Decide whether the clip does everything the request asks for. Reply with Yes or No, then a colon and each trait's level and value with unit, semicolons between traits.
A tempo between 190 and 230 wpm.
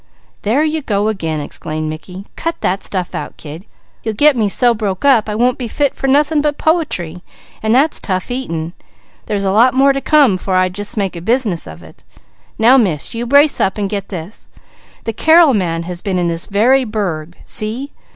Yes: average, 200 wpm